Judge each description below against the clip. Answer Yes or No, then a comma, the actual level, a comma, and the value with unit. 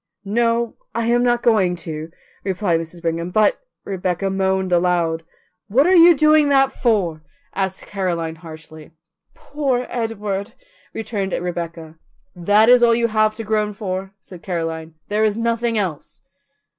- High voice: Yes, high, 195 Hz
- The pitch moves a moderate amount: Yes, average, 5.0 semitones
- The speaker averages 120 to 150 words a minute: Yes, average, 145 wpm